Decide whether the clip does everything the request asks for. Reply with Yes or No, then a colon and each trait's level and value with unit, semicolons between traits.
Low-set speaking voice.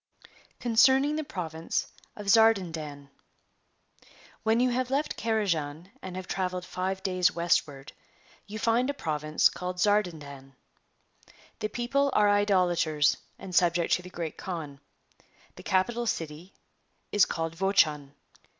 No: medium, 185 Hz